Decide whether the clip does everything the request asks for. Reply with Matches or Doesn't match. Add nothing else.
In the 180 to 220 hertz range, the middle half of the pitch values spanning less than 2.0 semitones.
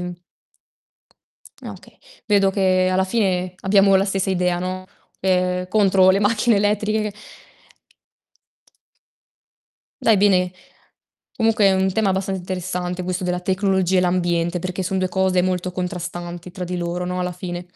Matches